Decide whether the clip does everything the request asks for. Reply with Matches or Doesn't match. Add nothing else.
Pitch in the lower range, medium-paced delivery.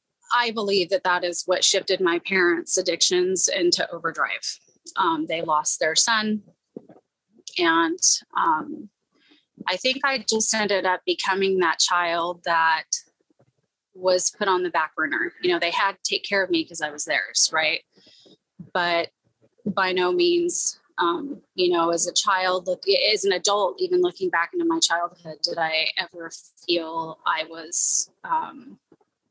Doesn't match